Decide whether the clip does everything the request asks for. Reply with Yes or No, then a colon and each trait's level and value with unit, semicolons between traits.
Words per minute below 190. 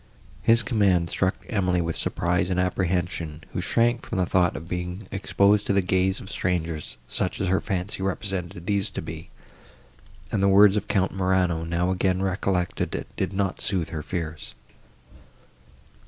Yes: average, 160 wpm